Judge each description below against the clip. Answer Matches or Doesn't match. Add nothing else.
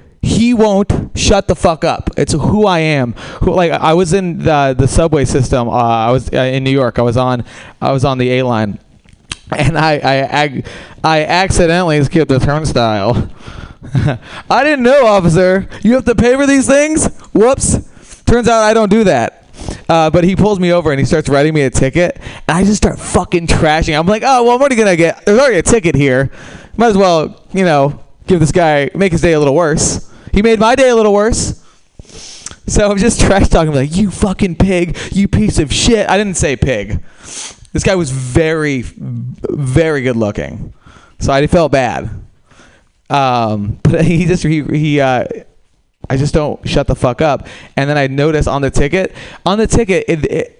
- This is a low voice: Doesn't match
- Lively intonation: Matches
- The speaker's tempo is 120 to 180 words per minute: Doesn't match